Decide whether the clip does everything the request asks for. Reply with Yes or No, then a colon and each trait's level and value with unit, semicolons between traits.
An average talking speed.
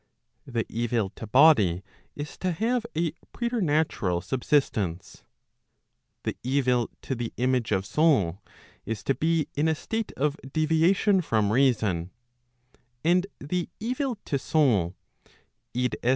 No: slow, 125 wpm